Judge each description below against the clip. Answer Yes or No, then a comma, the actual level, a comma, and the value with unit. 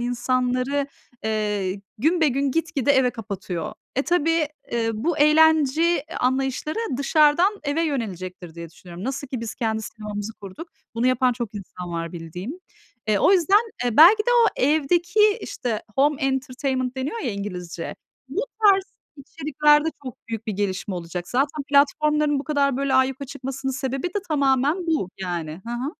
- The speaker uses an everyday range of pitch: No, wide, 5.7 semitones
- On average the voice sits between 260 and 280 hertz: Yes, very high, 265 Hz